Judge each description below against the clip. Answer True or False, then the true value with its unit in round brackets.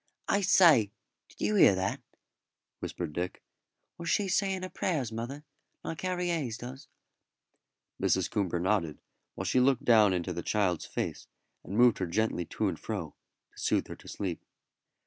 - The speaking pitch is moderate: False (110 Hz)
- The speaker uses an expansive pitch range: True (8.4 semitones)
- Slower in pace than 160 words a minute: False (165 wpm)